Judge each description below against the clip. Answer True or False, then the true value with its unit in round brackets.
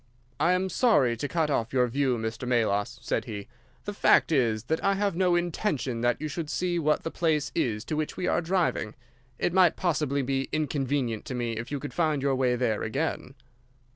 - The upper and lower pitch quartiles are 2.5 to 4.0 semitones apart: False (5.5 semitones)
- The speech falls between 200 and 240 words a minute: True (205 wpm)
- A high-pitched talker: False (140 Hz)